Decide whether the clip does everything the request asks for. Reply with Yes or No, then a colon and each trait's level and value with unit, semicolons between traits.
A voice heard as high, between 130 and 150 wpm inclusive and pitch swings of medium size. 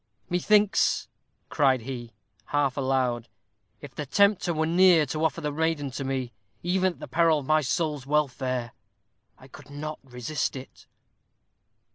No: medium, 145 Hz; average, 145 wpm; average, 3.6 semitones